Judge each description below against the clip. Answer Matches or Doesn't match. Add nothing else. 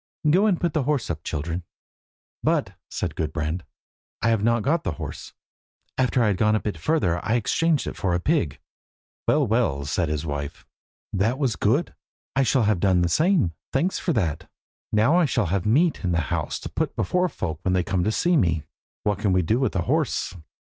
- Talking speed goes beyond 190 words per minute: Matches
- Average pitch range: Doesn't match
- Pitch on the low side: Matches